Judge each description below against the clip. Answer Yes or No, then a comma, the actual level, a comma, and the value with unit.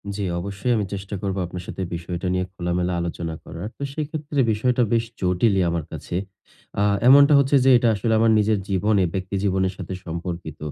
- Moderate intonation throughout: Yes, average, 4.3 semitones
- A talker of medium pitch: No, very low, 95 Hz